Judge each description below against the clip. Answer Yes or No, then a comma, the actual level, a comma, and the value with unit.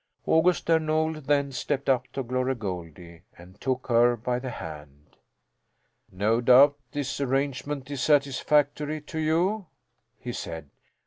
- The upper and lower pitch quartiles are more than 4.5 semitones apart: No, average, 4.1 semitones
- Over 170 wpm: No, slow, 135 wpm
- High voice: No, low, 135 Hz